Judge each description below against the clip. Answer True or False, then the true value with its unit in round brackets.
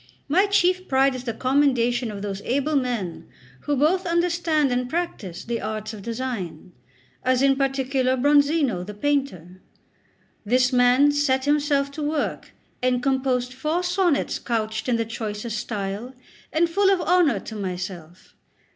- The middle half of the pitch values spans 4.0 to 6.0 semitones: True (4.7 semitones)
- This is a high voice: True (255 Hz)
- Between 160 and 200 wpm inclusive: False (145 wpm)